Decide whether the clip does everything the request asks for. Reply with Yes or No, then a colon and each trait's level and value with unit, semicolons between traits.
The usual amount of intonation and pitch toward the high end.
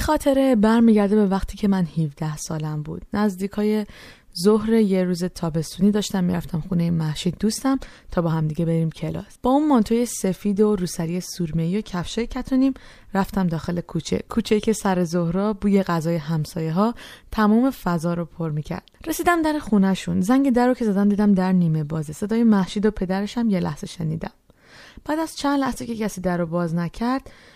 Yes: average, 4.5 semitones; high, 195 Hz